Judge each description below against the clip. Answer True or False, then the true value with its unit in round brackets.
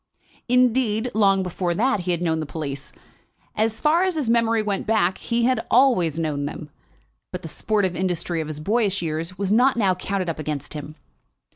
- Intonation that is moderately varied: False (5.7 semitones)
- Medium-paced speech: True (185 wpm)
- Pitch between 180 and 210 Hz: True (190 Hz)